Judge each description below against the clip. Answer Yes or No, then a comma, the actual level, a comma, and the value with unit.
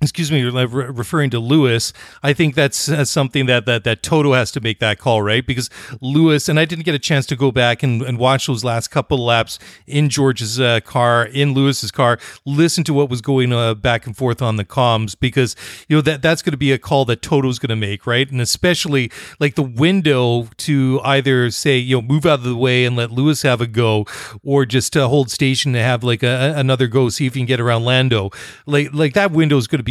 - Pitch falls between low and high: No, low, 130 Hz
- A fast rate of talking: Yes, fast, 235 wpm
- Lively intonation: No, average, 3.2 semitones